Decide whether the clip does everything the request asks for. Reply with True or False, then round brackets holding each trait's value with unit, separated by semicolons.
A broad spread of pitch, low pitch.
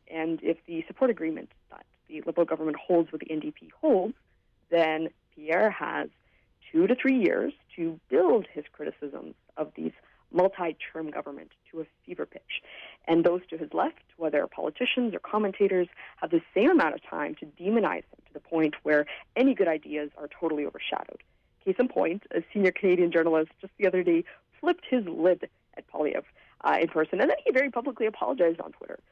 False (6.0 semitones; 170 Hz)